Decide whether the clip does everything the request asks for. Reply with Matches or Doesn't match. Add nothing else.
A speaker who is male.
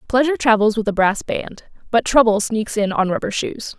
Doesn't match